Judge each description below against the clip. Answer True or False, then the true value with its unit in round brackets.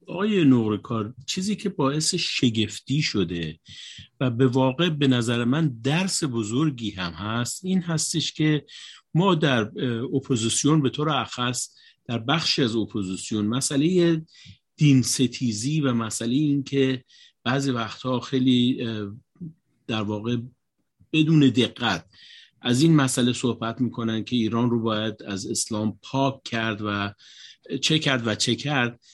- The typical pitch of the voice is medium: False (125 Hz)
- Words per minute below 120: False (130 wpm)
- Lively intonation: False (4.6 semitones)